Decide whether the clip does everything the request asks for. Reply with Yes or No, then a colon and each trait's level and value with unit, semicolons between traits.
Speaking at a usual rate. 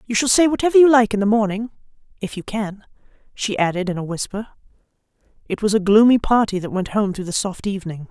No: fast, 215 wpm